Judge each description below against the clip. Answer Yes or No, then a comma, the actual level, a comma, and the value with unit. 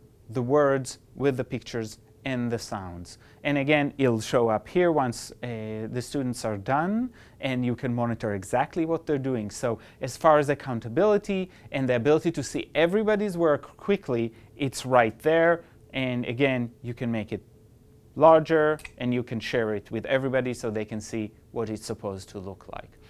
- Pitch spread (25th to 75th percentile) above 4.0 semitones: Yes, average, 4.6 semitones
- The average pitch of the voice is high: No, low, 125 Hz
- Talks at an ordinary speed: Yes, average, 175 wpm